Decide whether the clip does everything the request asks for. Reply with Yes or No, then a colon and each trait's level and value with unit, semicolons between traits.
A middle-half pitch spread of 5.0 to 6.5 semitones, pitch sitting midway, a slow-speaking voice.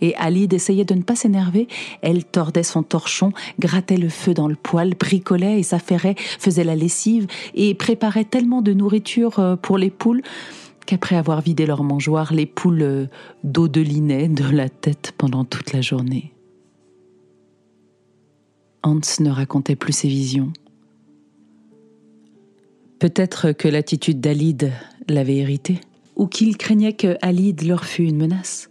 Yes: wide, 5.5 semitones; medium, 165 Hz; slow, 140 wpm